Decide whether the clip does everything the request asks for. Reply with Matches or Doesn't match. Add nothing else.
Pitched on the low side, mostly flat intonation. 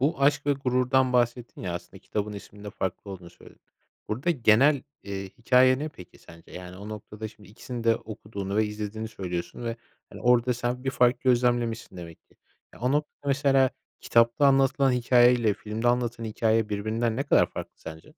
Doesn't match